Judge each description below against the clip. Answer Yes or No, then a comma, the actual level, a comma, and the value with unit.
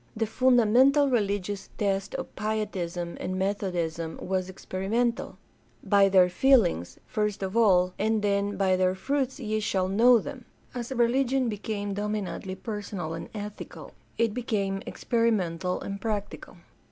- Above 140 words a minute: No, slow, 135 wpm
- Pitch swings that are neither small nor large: Yes, average, 3.5 semitones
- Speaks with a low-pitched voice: No, high, 205 Hz